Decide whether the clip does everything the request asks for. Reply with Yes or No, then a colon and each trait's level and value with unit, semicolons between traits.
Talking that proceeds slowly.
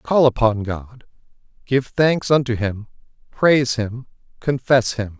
Yes: slow, 125 wpm